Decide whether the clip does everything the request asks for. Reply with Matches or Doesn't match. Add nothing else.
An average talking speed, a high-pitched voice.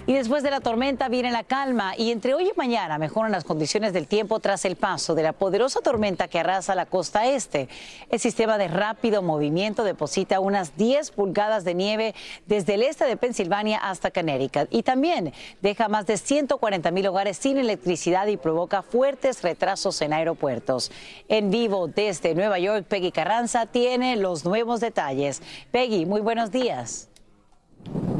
Matches